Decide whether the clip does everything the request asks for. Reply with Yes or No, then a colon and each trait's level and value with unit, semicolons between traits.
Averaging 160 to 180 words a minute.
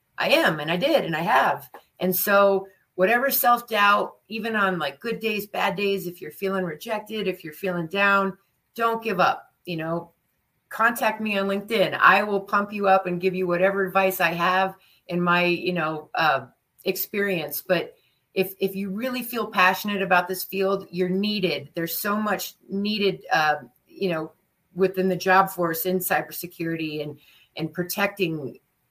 Yes: average, 170 wpm